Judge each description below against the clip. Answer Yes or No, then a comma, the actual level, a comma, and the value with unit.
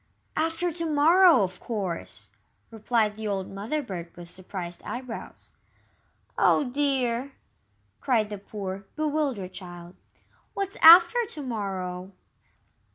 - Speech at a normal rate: No, slow, 110 wpm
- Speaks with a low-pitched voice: No, high, 225 Hz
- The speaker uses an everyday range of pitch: No, wide, 7.6 semitones